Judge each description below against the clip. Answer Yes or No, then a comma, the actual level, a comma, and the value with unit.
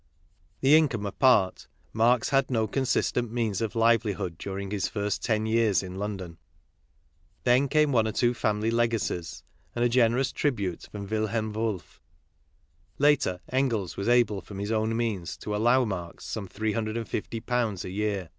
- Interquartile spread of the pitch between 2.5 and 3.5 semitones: Yes, average, 3.1 semitones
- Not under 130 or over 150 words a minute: No, average, 165 wpm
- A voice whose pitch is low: Yes, low, 110 Hz